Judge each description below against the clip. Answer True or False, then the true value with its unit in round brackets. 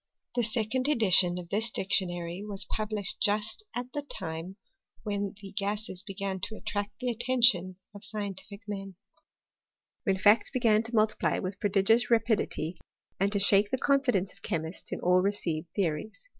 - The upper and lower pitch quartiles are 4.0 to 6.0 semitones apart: False (2.8 semitones)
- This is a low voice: False (205 Hz)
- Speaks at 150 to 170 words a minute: True (160 wpm)